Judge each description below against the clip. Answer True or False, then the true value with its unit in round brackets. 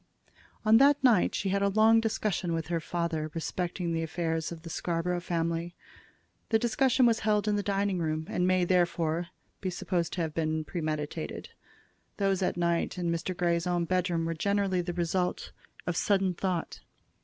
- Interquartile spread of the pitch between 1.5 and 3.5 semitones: True (2.9 semitones)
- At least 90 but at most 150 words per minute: False (175 wpm)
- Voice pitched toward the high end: False (175 Hz)